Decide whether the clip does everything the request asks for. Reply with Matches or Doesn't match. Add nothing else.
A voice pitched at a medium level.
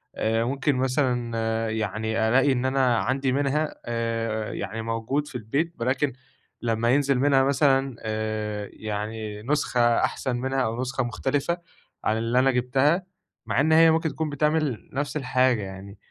Doesn't match